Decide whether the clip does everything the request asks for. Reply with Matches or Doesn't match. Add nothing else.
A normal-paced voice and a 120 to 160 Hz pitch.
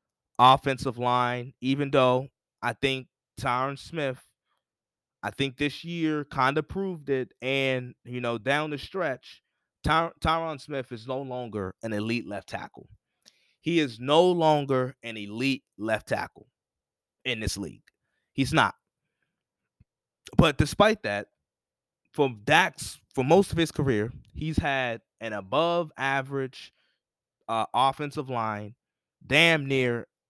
Doesn't match